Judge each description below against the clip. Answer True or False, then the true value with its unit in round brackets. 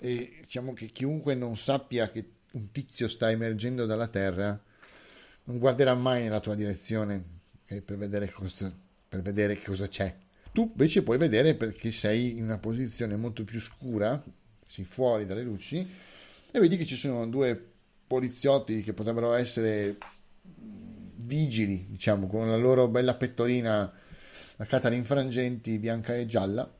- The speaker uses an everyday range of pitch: True (3.5 semitones)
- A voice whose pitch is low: True (115 Hz)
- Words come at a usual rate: True (150 wpm)